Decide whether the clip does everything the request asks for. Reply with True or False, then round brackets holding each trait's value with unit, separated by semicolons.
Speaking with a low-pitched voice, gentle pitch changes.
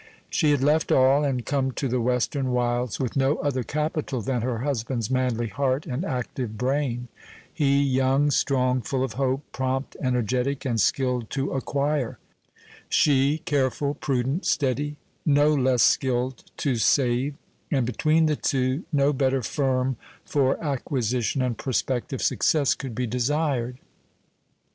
True (130 Hz; 2.2 semitones)